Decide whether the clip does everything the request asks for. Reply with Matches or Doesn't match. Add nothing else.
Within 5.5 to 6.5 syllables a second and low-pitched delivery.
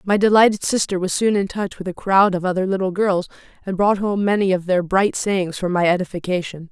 Doesn't match